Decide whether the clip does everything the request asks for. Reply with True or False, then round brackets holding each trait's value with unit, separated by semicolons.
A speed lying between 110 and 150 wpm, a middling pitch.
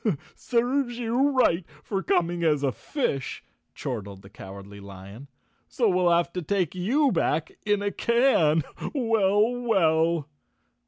True (140 wpm; 180 Hz)